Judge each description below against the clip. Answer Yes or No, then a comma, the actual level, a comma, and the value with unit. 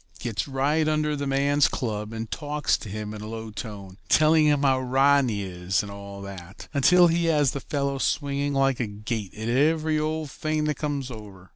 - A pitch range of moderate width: No, wide, 5.8 semitones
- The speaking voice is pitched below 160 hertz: Yes, low, 135 Hz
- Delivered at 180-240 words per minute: Yes, fast, 205 wpm